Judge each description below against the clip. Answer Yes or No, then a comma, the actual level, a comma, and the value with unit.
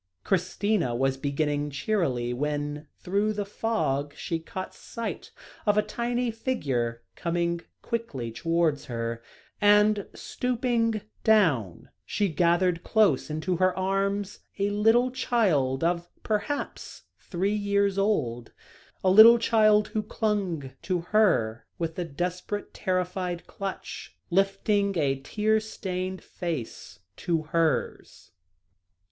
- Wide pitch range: Yes, wide, 5.9 semitones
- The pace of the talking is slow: Yes, slow, 115 wpm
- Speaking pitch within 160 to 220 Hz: Yes, medium, 185 Hz